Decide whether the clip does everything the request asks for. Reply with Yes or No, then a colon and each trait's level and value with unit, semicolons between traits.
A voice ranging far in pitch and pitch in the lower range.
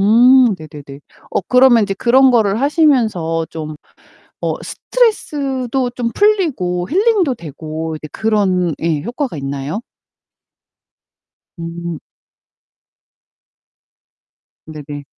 No: wide, 8.4 semitones; high, 210 Hz